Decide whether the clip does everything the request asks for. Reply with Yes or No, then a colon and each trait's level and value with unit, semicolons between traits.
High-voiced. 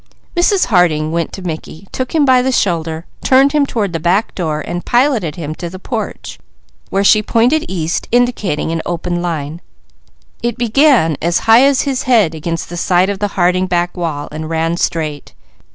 No: medium, 180 Hz